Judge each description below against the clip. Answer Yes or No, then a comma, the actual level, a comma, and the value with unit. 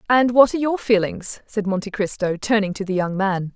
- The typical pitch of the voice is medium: No, high, 205 Hz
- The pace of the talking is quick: Yes, fast, 220 wpm